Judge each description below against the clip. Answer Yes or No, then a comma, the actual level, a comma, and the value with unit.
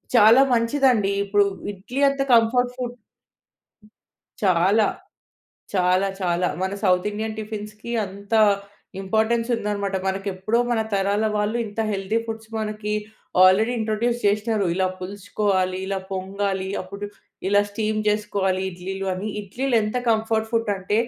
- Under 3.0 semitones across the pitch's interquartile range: Yes, narrow, 2.5 semitones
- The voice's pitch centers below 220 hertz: Yes, high, 205 Hz